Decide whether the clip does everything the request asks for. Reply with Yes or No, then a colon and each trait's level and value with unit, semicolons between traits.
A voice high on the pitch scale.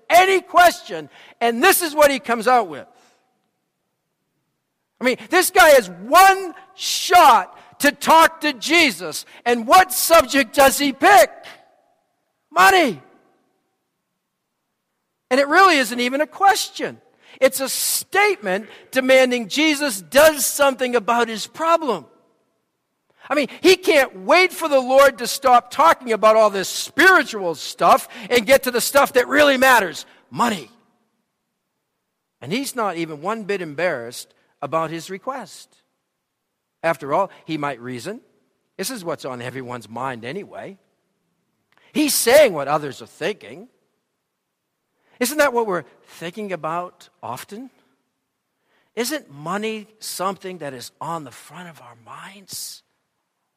Yes: very high, 255 Hz